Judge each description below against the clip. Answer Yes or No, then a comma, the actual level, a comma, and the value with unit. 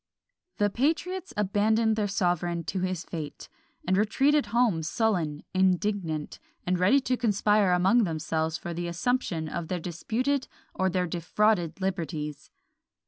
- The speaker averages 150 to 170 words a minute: No, slow, 135 wpm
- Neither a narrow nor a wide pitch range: Yes, average, 4.4 semitones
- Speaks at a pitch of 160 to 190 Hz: Yes, medium, 185 Hz